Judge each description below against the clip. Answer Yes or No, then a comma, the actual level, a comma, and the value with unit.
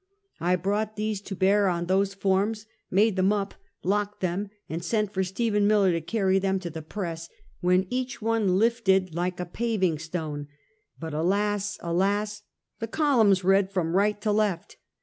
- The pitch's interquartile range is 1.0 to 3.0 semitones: Yes, narrow, 2.6 semitones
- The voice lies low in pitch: No, high, 195 Hz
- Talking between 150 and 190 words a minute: Yes, average, 170 wpm